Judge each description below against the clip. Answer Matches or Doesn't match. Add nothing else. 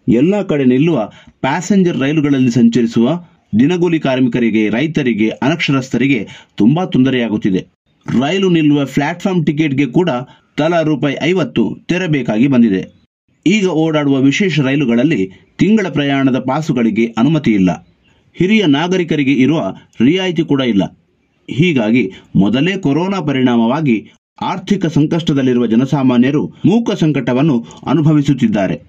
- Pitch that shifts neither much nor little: Matches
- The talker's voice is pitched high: Doesn't match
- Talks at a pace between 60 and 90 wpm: Doesn't match